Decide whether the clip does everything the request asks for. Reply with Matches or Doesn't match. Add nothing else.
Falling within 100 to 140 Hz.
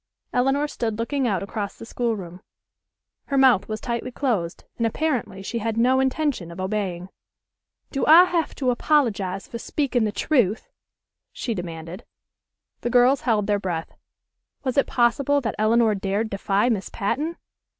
Doesn't match